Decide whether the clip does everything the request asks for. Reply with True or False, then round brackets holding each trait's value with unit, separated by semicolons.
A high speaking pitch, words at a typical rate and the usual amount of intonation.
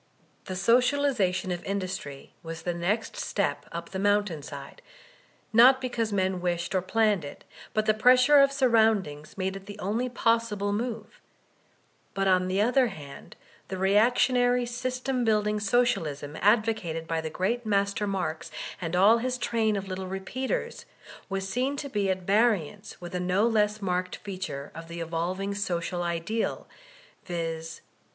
True (200 Hz; 160 wpm; 4.4 semitones)